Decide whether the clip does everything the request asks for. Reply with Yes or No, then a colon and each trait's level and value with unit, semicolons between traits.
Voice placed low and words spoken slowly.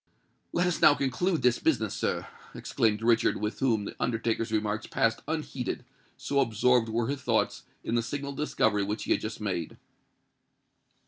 No: low, 115 Hz; average, 165 wpm